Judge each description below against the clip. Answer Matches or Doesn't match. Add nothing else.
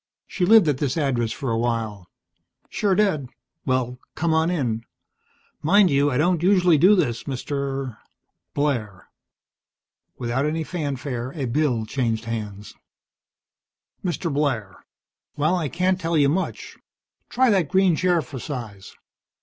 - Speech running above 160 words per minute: Doesn't match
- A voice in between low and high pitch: Matches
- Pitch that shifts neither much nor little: Doesn't match